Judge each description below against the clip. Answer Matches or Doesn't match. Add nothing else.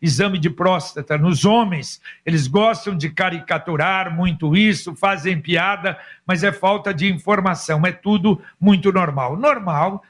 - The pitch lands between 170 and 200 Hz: Matches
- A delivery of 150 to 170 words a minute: Doesn't match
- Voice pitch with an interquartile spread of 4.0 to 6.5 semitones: Doesn't match